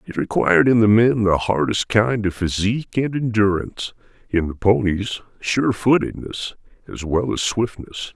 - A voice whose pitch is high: No, low, 105 Hz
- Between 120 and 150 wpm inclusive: Yes, average, 145 wpm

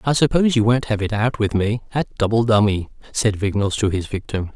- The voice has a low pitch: Yes, low, 110 Hz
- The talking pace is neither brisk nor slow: No, fast, 225 wpm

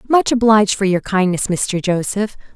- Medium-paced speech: Yes, average, 165 wpm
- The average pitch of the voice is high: Yes, high, 200 Hz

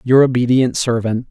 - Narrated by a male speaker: Yes, male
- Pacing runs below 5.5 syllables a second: Yes, 5.0 syllables/s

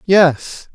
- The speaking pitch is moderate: Yes, medium, 170 Hz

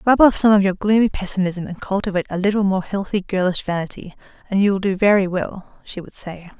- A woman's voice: Yes, female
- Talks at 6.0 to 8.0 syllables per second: Yes, 6.1 syllables/s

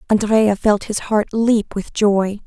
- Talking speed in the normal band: Yes, average, 170 wpm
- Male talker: No, female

